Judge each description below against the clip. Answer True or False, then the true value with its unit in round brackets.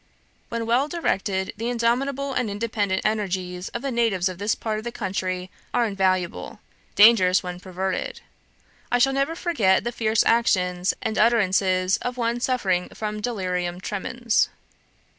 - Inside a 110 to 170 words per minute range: True (145 wpm)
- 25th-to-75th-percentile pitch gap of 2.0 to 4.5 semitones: True (4.2 semitones)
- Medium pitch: False (215 Hz)